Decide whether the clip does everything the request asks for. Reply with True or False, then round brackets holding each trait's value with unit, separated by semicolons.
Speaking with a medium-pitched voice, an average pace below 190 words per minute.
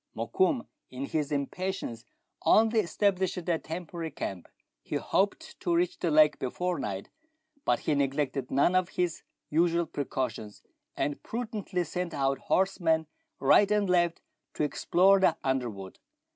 True (165 Hz; 140 wpm)